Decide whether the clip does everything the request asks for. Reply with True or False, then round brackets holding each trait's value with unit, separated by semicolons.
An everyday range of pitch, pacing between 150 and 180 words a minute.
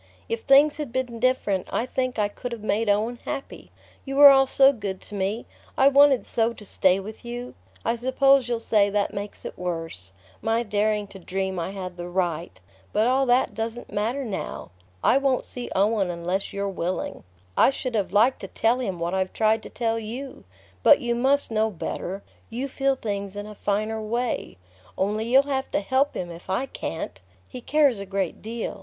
False (4.5 semitones; 195 wpm)